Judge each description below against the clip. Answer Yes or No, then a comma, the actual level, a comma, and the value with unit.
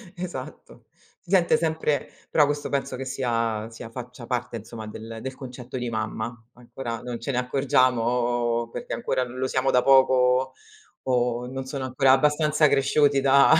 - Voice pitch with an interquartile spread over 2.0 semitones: Yes, narrow, 2.4 semitones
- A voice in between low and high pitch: No, low, 130 Hz